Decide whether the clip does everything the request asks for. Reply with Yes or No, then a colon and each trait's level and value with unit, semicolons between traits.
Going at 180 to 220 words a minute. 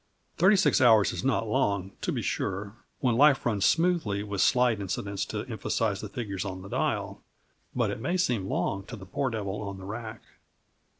Yes: average, 190 wpm